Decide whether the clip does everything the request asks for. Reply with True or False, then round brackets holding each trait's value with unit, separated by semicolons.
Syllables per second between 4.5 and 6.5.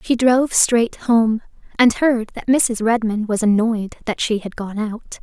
False (4.1 syllables/s)